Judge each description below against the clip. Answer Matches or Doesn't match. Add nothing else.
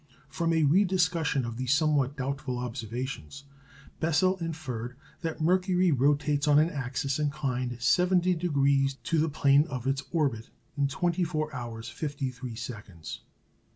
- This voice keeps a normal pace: Doesn't match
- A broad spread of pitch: Doesn't match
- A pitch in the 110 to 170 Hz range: Matches